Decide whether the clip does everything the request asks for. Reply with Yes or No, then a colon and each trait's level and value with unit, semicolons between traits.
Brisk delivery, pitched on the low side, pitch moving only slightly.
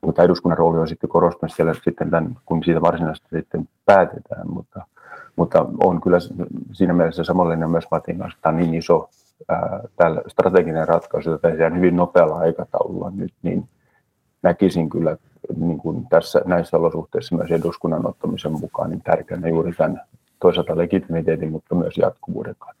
Yes: fast, 160 wpm; very low, 85 Hz; narrow, 1.0 semitones